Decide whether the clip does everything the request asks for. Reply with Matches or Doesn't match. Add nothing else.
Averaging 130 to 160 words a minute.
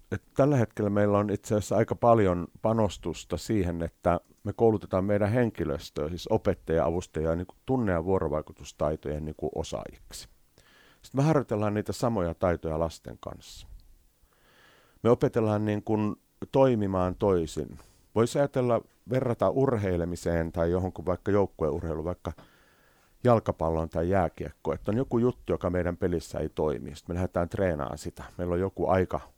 Matches